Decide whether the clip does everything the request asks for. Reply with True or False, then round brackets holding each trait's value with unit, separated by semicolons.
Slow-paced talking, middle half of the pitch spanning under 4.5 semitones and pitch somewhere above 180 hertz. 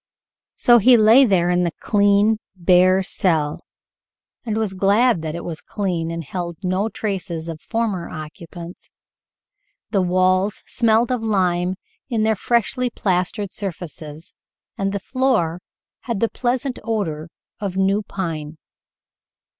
True (130 wpm; 4.1 semitones; 190 Hz)